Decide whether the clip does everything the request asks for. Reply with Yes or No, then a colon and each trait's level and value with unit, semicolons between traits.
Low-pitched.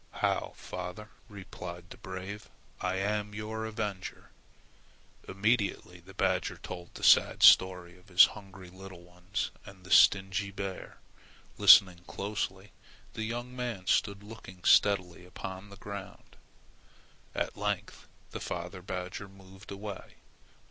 Yes: very low, 95 Hz